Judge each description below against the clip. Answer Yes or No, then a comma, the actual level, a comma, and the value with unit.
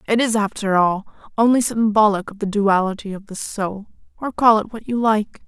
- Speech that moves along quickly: No, average, 185 wpm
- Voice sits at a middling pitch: No, high, 210 Hz